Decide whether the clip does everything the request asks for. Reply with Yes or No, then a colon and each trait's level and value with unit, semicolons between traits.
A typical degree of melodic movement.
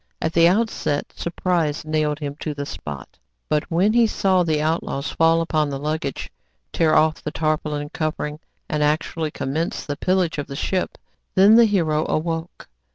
No: narrow, 2.2 semitones